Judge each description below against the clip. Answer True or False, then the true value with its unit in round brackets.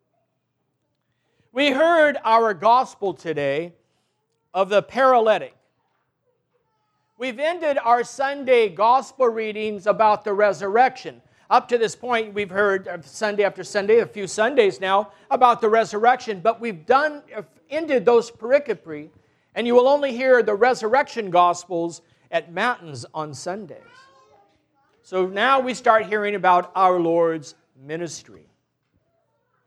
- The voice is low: False (215 Hz)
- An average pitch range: False (5.9 semitones)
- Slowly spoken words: True (120 wpm)